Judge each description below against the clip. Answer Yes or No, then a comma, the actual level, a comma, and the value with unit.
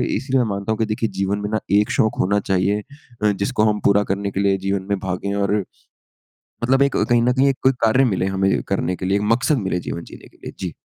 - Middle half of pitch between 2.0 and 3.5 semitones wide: Yes, average, 3.2 semitones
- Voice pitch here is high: No, low, 100 Hz